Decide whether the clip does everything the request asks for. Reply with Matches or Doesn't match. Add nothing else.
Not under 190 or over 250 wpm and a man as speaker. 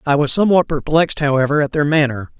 Matches